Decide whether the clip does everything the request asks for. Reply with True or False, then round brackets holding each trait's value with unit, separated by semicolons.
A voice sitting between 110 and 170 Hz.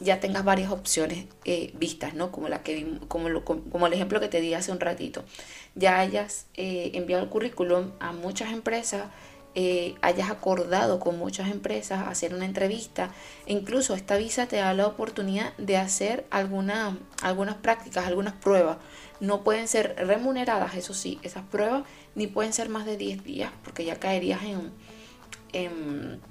False (190 Hz)